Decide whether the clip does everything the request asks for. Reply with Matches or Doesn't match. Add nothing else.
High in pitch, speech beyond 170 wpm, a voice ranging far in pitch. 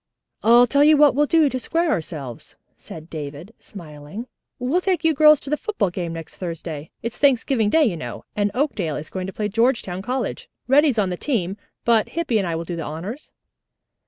Matches